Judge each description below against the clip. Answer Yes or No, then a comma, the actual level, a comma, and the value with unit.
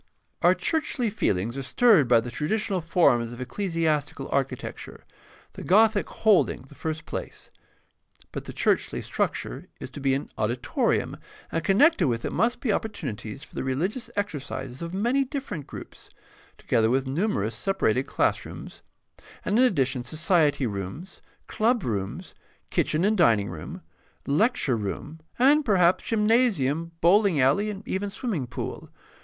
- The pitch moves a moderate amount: No, wide, 8.2 semitones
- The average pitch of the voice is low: No, medium, 160 Hz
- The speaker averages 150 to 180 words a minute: No, average, 140 wpm